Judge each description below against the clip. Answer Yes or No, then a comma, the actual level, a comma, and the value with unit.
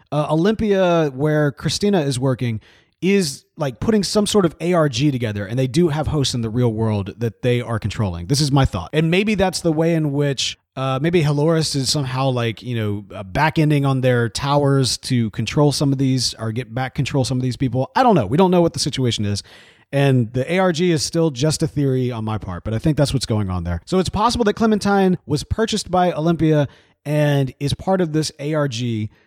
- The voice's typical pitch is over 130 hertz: Yes, medium, 140 Hz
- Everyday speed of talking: No, fast, 220 wpm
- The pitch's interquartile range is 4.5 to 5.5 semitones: Yes, average, 5.1 semitones